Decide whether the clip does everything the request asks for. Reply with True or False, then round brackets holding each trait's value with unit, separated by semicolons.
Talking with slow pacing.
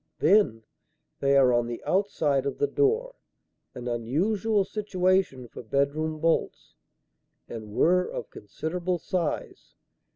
True (120 wpm)